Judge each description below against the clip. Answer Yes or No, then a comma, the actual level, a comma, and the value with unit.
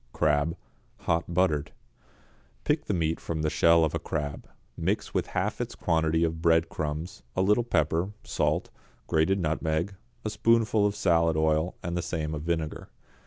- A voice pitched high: No, very low, 80 Hz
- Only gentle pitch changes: Yes, narrow, 2.0 semitones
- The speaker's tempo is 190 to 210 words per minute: No, average, 160 wpm